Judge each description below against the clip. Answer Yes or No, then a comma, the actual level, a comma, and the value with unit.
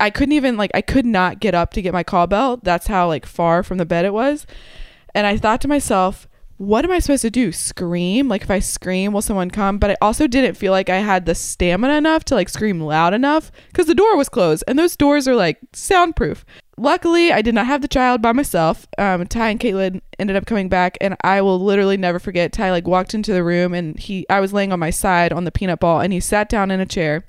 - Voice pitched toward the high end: Yes, high, 195 Hz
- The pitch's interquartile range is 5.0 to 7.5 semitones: Yes, wide, 5.6 semitones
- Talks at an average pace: No, fast, 255 wpm